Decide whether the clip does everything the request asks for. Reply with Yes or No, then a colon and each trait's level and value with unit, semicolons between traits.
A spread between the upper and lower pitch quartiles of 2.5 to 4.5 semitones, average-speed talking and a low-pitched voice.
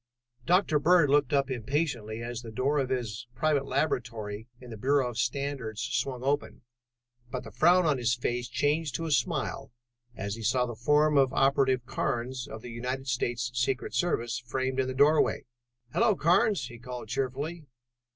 Yes: average, 3.2 semitones; average, 175 wpm; low, 130 Hz